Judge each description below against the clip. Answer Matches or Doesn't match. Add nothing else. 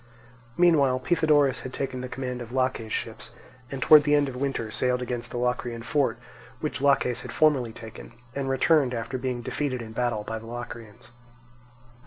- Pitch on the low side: Matches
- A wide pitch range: Doesn't match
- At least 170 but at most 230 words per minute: Matches